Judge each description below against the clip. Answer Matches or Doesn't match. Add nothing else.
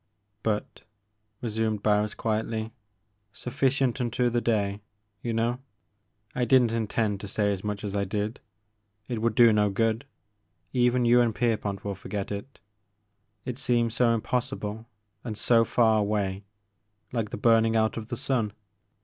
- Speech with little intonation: Matches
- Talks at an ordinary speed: Matches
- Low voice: Matches